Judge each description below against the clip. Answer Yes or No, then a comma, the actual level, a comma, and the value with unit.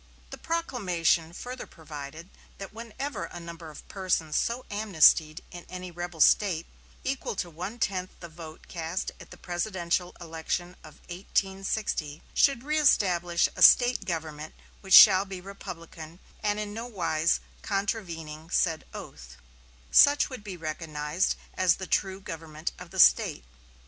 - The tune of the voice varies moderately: Yes, average, 3.8 semitones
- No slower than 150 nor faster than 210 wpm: No, average, 140 wpm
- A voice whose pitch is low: No, medium, 175 Hz